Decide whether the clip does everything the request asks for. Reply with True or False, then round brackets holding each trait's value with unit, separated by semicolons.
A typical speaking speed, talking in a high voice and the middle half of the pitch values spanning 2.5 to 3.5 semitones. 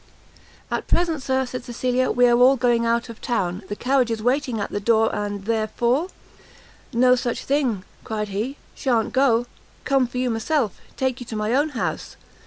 True (190 wpm; 245 Hz; 2.8 semitones)